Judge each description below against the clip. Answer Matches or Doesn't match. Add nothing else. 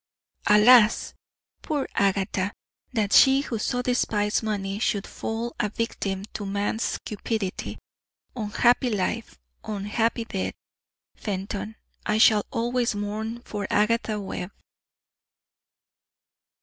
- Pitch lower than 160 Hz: Doesn't match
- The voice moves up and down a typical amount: Doesn't match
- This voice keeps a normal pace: Doesn't match